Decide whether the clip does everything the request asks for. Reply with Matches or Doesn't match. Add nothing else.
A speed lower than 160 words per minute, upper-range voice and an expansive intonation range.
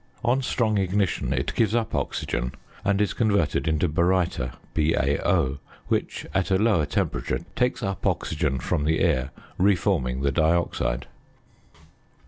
Doesn't match